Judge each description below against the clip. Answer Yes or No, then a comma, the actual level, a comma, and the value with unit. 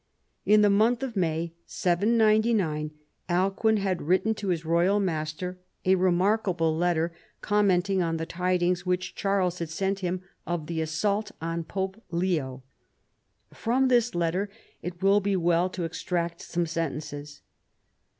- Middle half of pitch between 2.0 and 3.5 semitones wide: Yes, average, 3.1 semitones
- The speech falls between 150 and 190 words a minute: No, average, 140 wpm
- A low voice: No, medium, 180 Hz